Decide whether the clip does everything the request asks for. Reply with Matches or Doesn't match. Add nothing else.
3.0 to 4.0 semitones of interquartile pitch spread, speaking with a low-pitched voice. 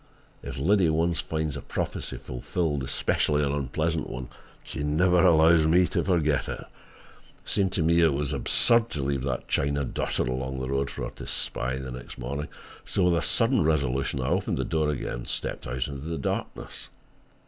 Matches